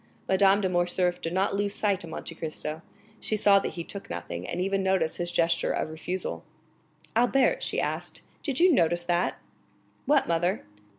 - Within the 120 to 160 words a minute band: No, average, 175 wpm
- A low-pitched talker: No, medium, 185 Hz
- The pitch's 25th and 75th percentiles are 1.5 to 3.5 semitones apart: Yes, average, 2.7 semitones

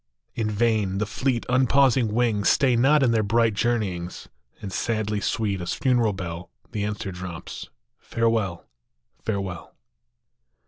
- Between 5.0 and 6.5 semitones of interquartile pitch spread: No, average, 3.3 semitones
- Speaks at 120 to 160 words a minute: Yes, slow, 135 wpm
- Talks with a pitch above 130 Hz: No, low, 110 Hz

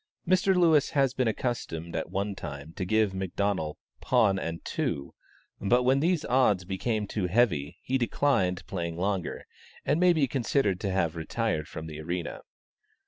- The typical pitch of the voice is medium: No, low, 100 Hz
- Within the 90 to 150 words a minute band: No, average, 160 wpm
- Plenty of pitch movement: Yes, wide, 6.9 semitones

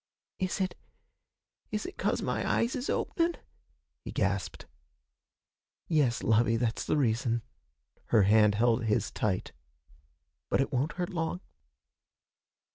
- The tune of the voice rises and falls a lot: Yes, wide, 8.1 semitones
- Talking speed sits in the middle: No, slow, 120 wpm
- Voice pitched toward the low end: Yes, low, 125 Hz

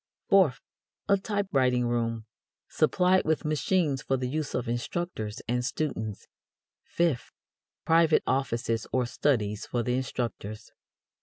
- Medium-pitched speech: No, low, 130 Hz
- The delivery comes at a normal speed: No, slow, 120 wpm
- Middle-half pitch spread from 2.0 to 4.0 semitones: No, average, 5.0 semitones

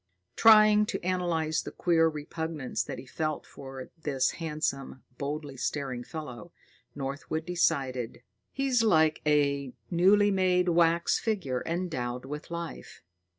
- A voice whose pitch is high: No, medium, 160 Hz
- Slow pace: Yes, slow, 120 wpm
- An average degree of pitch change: Yes, average, 4.4 semitones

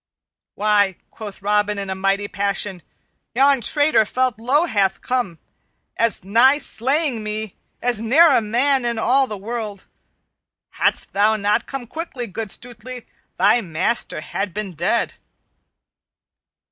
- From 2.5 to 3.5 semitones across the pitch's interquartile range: No, average, 3.9 semitones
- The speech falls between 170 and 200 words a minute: No, slow, 135 wpm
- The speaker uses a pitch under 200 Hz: No, high, 220 Hz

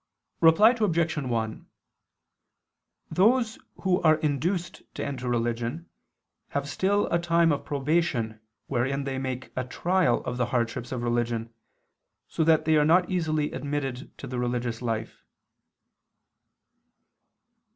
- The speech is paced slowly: Yes, slow, 125 wpm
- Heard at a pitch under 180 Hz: Yes, medium, 140 Hz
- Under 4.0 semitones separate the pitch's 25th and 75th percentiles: No, wide, 5.6 semitones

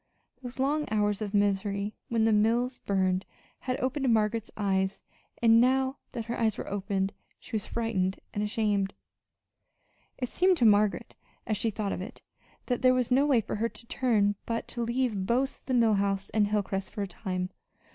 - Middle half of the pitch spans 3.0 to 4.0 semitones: Yes, average, 3.4 semitones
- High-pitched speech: Yes, high, 220 Hz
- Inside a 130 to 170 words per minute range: No, average, 185 wpm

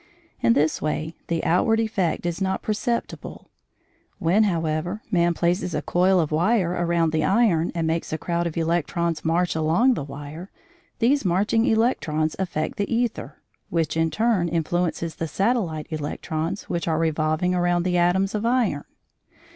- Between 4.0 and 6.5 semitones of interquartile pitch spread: No, average, 3.4 semitones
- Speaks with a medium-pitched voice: Yes, medium, 170 Hz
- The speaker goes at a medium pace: Yes, average, 155 wpm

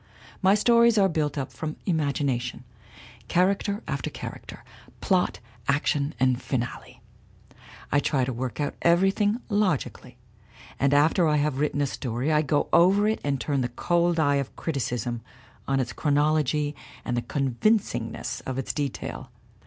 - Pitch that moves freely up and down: No, average, 4.7 semitones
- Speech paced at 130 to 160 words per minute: Yes, average, 150 wpm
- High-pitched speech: No, medium, 145 Hz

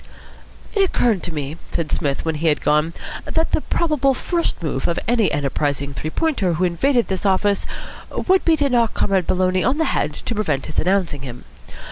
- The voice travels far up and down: Yes, wide, 8.6 semitones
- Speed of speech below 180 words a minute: No, average, 190 wpm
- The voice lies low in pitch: No, medium, 185 Hz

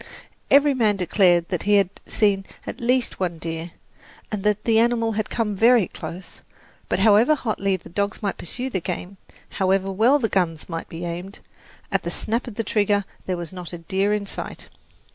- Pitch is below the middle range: No, high, 200 Hz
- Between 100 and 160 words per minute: No, average, 190 wpm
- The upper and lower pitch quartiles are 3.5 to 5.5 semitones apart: Yes, average, 3.8 semitones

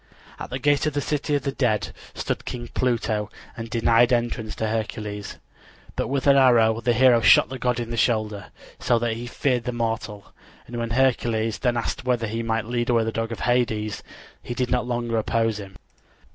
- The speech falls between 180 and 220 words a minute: Yes, average, 200 wpm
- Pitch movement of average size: No, narrow, 1.8 semitones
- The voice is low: Yes, low, 115 Hz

